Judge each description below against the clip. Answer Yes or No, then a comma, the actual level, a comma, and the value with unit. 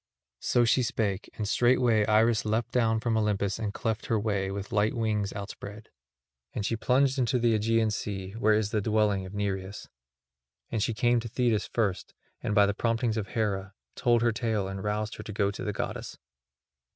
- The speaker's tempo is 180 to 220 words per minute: Yes, average, 190 wpm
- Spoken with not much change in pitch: Yes, narrow, 2.0 semitones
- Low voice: Yes, low, 110 Hz